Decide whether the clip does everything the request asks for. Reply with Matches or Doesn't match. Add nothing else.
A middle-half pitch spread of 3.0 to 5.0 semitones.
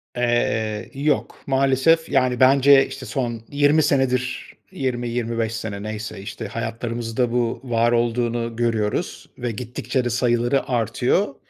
Doesn't match